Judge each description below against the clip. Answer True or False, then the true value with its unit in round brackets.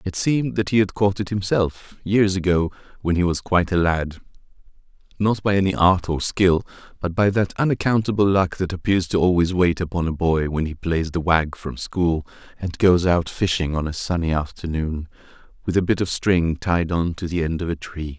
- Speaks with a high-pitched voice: False (90 Hz)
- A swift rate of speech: True (210 wpm)